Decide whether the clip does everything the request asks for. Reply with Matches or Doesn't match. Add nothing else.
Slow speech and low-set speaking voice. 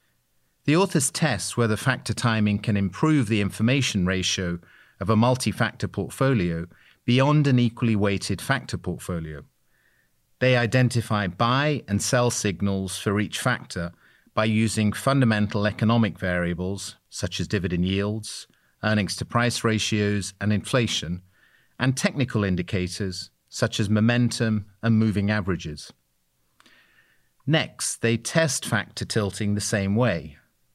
Matches